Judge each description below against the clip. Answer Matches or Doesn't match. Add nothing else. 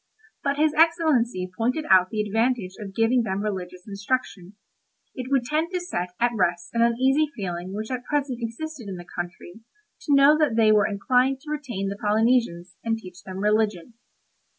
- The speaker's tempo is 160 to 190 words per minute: Matches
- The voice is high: Matches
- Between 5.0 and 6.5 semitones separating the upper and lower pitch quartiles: Matches